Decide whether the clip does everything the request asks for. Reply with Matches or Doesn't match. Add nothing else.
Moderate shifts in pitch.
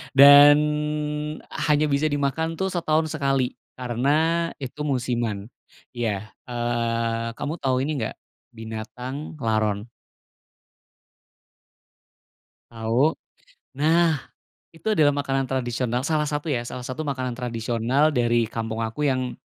Matches